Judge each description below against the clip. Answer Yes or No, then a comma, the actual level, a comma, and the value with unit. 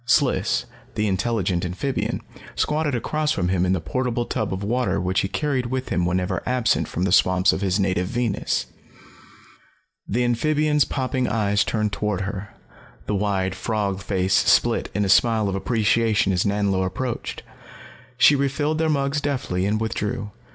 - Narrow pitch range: No, average, 5.0 semitones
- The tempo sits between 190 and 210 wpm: No, average, 160 wpm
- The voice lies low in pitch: Yes, low, 105 Hz